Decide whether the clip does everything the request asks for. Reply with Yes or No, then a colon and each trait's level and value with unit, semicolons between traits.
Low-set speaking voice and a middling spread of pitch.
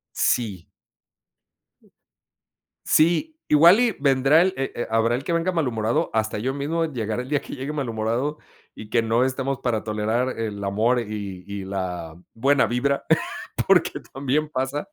Yes: low, 125 Hz; average, 4.7 semitones